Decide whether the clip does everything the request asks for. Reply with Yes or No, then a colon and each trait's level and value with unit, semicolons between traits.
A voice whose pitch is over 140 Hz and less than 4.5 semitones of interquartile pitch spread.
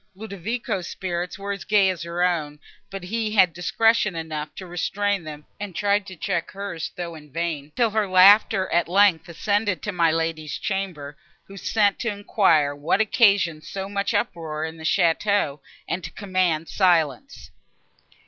Yes: medium, 185 Hz; average, 3.7 semitones